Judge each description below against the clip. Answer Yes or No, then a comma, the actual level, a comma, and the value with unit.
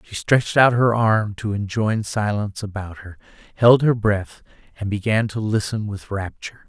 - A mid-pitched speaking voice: No, low, 105 Hz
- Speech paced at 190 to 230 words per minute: No, average, 170 wpm